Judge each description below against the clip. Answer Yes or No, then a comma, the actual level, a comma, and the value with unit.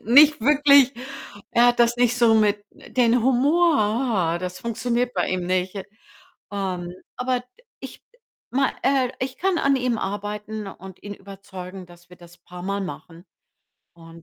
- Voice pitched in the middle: No, high, 220 Hz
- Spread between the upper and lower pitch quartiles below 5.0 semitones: No, average, 5.3 semitones